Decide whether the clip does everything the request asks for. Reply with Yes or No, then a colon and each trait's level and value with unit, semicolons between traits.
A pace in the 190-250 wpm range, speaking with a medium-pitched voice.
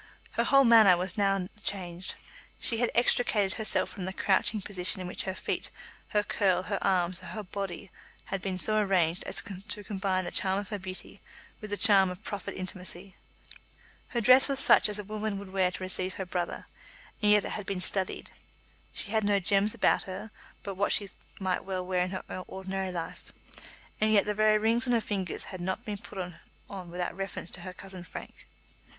No: average, 200 wpm; high, 195 Hz